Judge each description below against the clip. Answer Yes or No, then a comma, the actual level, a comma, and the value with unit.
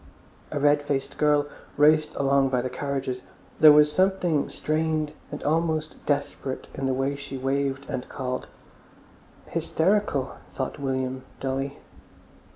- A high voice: No, medium, 140 Hz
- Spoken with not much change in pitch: Yes, narrow, 2.2 semitones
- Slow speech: Yes, slow, 130 wpm